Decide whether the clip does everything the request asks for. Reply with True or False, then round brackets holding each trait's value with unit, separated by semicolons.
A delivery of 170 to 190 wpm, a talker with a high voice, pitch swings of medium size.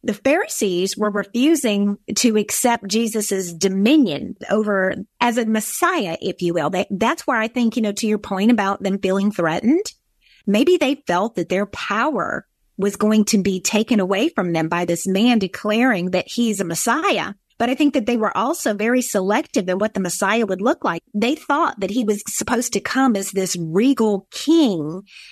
True (185 wpm; 215 Hz; 3.8 semitones)